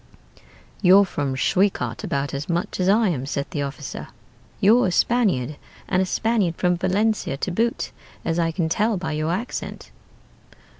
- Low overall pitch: No, medium, 180 Hz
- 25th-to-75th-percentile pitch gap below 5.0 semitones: No, wide, 5.6 semitones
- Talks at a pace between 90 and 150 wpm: No, average, 160 wpm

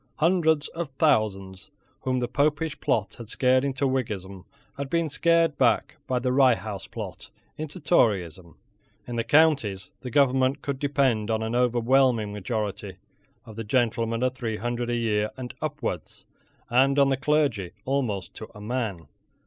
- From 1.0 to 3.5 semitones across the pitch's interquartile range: No, average, 4.3 semitones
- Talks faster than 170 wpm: No, average, 155 wpm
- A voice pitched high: No, low, 125 Hz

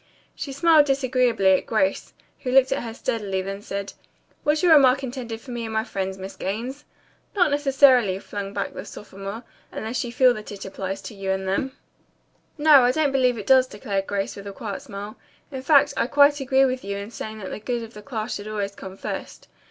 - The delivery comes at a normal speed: No, fast, 215 wpm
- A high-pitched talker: Yes, high, 230 Hz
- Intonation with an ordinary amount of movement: Yes, average, 4.9 semitones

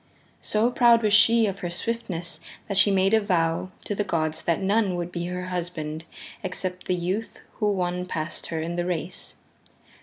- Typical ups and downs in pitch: Yes, average, 3.1 semitones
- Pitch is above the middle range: No, medium, 180 Hz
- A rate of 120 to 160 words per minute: No, average, 185 wpm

